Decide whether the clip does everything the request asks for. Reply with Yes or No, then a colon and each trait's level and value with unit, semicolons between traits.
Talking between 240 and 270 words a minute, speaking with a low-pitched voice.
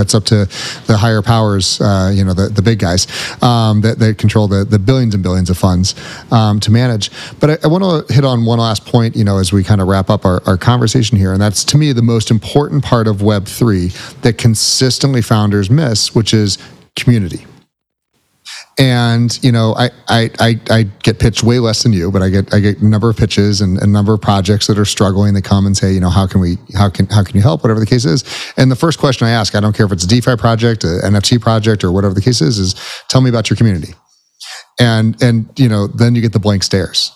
Yes: fast, 245 wpm; low, 110 Hz